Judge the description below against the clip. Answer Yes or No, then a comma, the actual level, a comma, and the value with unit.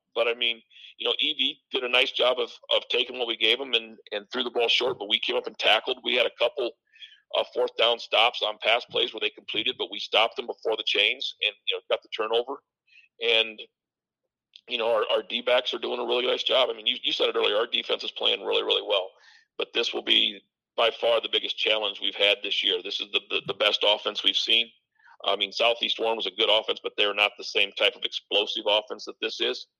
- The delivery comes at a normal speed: No, fast, 250 wpm